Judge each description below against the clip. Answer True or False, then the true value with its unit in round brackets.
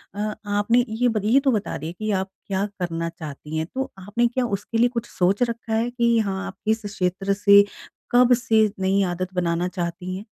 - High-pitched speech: True (205 Hz)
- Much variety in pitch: False (4.0 semitones)